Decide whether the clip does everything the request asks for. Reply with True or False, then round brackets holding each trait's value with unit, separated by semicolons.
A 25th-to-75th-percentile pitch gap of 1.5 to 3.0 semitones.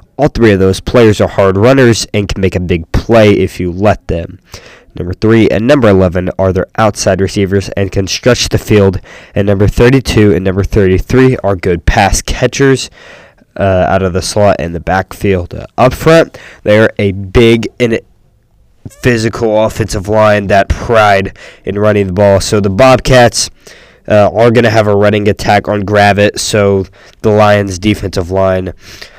True (2.6 semitones)